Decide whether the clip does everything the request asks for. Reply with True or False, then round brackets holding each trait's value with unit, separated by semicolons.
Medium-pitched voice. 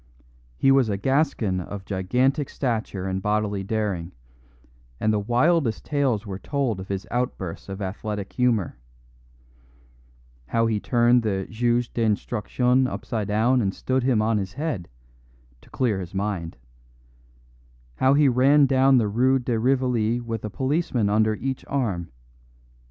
False (115 Hz)